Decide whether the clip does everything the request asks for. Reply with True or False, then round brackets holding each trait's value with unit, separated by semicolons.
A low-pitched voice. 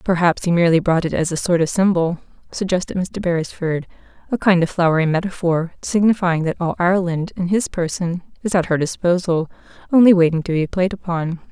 False (175 Hz)